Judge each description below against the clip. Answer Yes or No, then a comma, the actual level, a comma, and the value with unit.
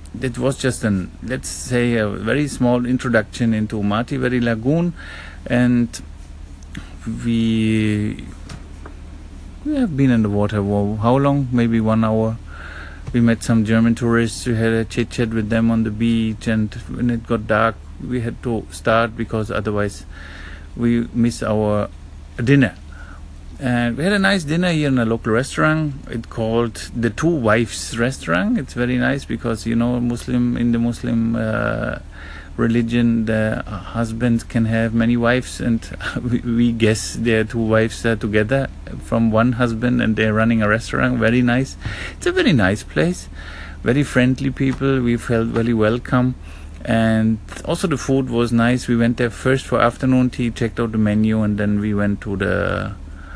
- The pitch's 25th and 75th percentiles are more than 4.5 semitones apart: No, average, 2.7 semitones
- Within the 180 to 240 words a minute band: No, average, 165 wpm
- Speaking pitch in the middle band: No, low, 115 Hz